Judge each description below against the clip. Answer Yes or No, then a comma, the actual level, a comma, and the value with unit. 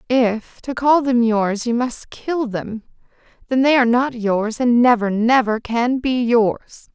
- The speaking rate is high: No, average, 175 wpm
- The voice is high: Yes, high, 240 Hz